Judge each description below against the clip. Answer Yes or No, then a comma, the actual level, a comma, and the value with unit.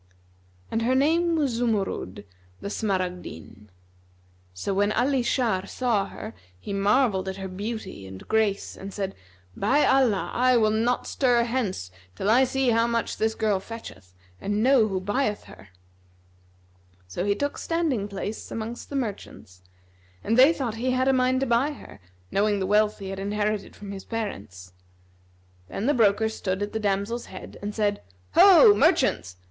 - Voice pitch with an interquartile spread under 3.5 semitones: No, average, 4.1 semitones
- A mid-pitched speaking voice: No, high, 215 Hz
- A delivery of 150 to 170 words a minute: Yes, average, 165 wpm